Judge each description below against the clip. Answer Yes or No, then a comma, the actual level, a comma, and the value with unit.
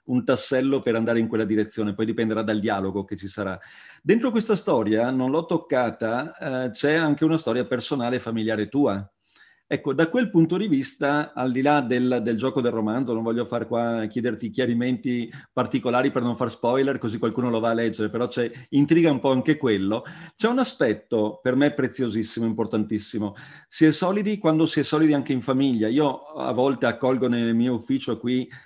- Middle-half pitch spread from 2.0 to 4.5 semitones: Yes, average, 3.8 semitones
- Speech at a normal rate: No, fast, 195 wpm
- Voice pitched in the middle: No, low, 125 Hz